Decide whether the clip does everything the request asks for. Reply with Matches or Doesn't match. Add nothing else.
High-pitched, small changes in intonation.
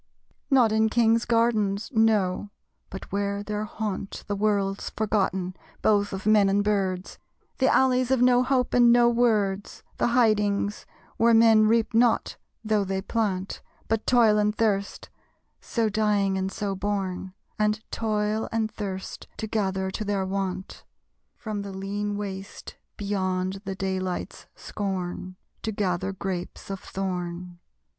Matches